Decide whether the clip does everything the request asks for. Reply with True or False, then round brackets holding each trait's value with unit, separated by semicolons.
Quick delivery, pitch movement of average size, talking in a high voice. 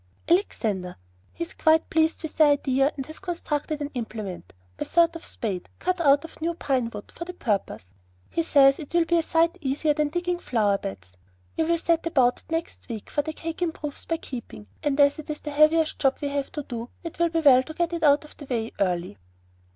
True (225 wpm; 4.5 semitones; 295 Hz)